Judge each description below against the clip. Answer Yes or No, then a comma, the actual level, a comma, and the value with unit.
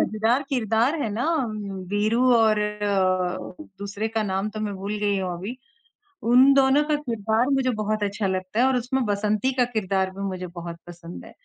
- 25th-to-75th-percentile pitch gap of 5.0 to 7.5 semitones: No, average, 3.9 semitones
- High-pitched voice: Yes, high, 215 Hz